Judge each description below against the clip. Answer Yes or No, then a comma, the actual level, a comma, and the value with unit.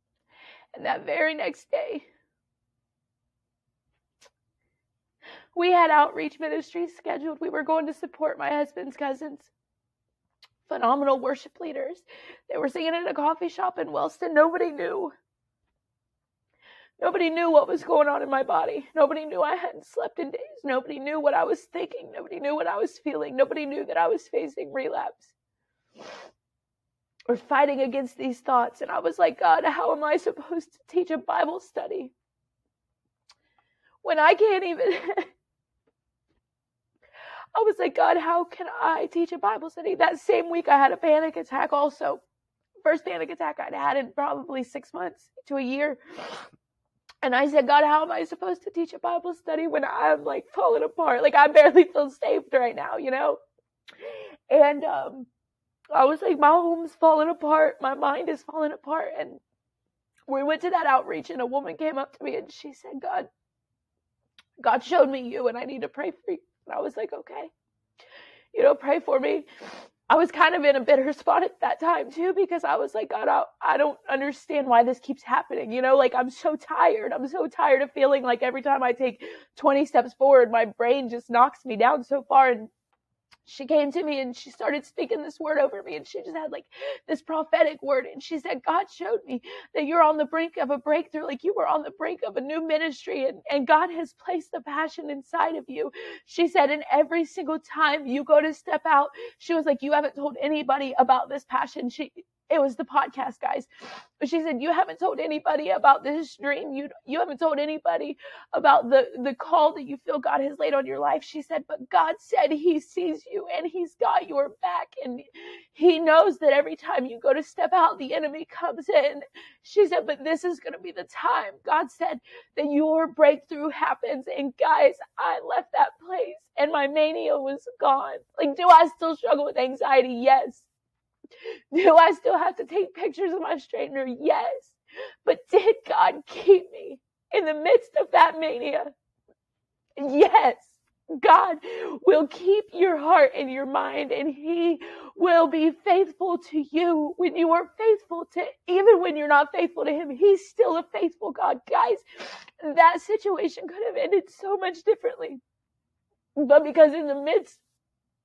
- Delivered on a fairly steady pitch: No, average, 3.9 semitones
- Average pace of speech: Yes, average, 190 wpm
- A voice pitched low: No, very high, 310 Hz